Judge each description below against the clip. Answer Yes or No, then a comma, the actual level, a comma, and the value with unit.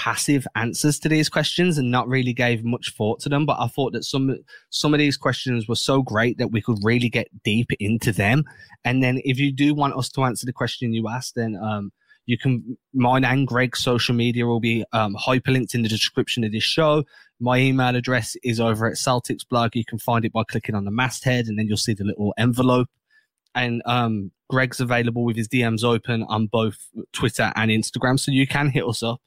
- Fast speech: Yes, fast, 220 wpm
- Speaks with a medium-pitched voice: No, low, 120 Hz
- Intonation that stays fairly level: Yes, narrow, 2.3 semitones